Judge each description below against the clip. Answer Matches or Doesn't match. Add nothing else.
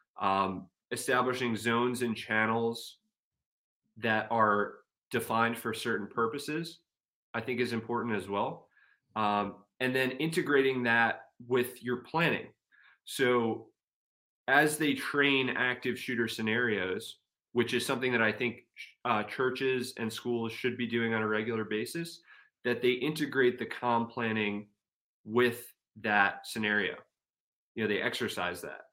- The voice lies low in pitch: Matches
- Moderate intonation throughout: Doesn't match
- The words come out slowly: Matches